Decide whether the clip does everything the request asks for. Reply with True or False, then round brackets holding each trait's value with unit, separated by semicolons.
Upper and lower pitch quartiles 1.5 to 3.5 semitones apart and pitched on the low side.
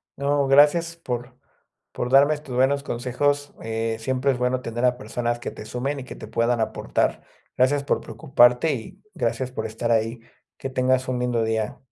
True (2.7 semitones; 125 Hz)